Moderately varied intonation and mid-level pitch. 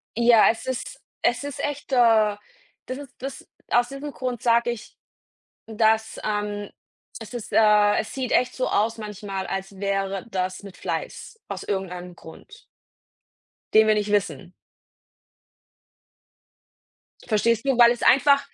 No: average, 3.2 semitones; high, 220 Hz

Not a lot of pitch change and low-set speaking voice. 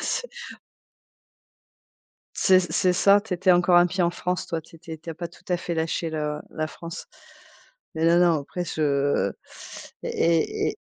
No: narrow, 2.0 semitones; medium, 170 Hz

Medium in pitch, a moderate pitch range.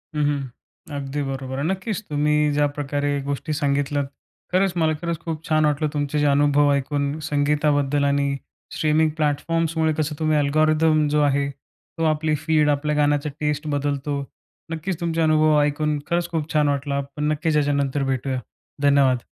No: medium, 150 Hz; narrow, 1.6 semitones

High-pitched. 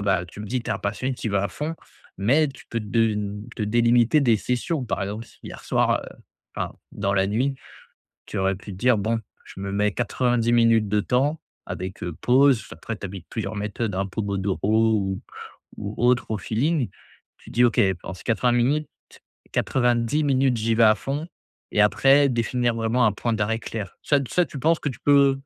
No: low, 115 Hz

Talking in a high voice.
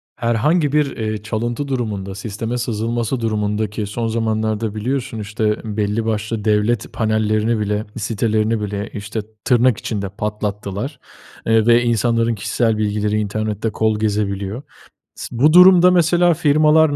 No: low, 110 Hz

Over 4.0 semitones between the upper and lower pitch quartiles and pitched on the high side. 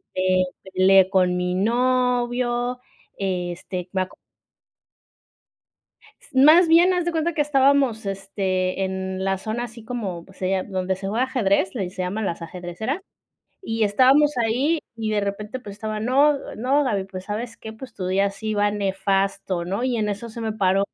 Yes: average, 4.7 semitones; high, 210 Hz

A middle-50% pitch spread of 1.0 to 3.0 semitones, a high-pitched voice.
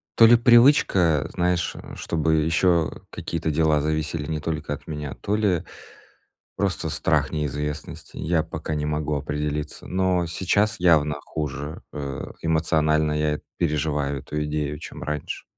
No: narrow, 2.4 semitones; very low, 75 Hz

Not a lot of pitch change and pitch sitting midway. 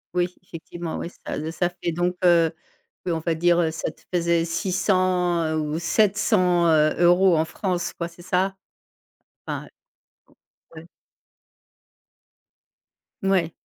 Yes: narrow, 1.6 semitones; medium, 175 Hz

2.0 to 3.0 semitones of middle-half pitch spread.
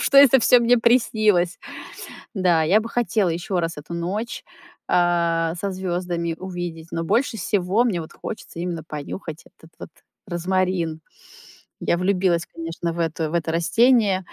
No: average, 3.6 semitones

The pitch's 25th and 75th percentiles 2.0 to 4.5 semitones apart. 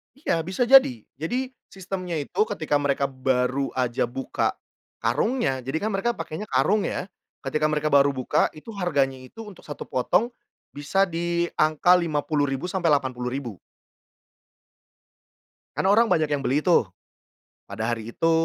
No: wide, 5.5 semitones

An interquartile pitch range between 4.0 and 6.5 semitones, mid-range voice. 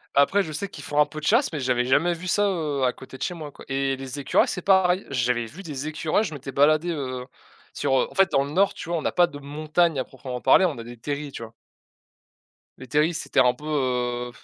Yes: average, 4.4 semitones; medium, 145 Hz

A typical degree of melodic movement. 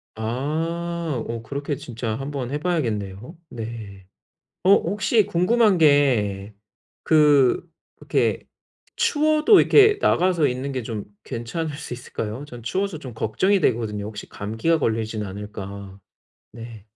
No: wide, 7.1 semitones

